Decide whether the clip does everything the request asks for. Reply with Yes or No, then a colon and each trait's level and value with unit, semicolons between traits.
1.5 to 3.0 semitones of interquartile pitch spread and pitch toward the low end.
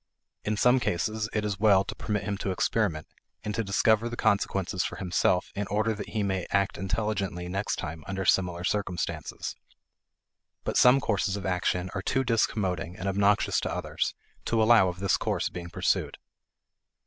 Yes: average, 2.7 semitones; low, 100 Hz